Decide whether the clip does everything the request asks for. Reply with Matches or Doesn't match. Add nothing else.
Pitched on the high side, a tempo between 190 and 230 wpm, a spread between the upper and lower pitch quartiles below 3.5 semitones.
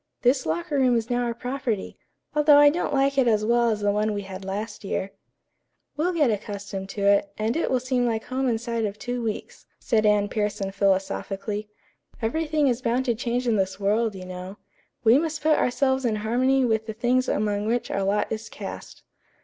Doesn't match